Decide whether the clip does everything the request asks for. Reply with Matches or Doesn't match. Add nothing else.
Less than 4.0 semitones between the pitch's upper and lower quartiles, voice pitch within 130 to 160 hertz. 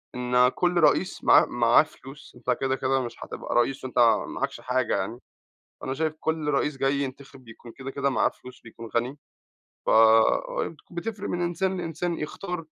Doesn't match